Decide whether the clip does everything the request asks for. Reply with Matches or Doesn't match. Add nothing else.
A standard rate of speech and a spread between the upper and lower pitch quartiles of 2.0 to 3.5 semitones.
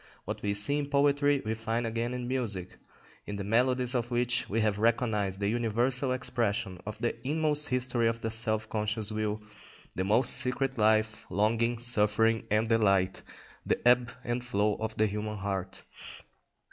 Matches